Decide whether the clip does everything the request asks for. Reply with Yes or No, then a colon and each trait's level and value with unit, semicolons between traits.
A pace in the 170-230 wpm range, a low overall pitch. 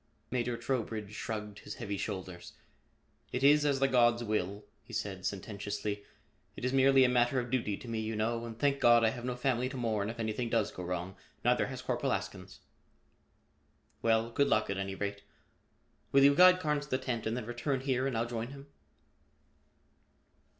Yes: average, 190 wpm; low, 115 Hz